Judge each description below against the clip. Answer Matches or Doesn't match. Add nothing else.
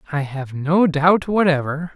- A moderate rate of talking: Matches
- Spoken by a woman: Doesn't match